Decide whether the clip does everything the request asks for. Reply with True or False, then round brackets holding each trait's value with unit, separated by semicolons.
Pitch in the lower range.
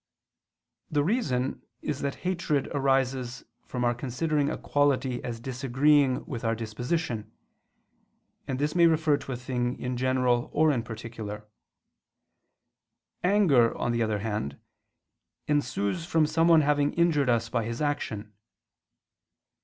True (130 Hz)